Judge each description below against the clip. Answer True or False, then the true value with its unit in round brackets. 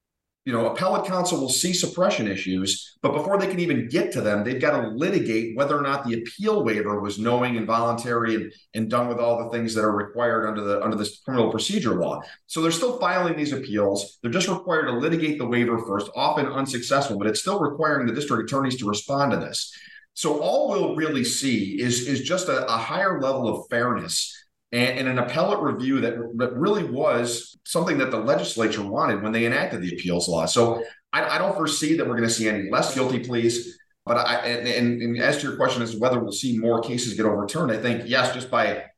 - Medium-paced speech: False (225 wpm)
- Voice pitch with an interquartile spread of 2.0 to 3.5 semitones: False (4.2 semitones)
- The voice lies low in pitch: True (120 Hz)